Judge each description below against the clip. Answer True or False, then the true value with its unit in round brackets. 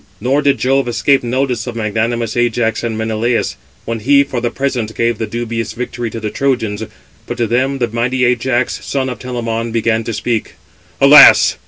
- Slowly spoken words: False (180 wpm)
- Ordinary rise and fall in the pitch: False (2.0 semitones)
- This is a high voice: False (120 Hz)